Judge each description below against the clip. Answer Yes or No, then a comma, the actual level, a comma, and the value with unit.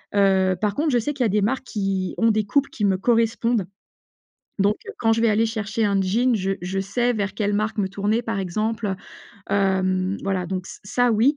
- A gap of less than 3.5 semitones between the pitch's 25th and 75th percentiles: Yes, average, 2.9 semitones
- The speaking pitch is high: Yes, high, 210 Hz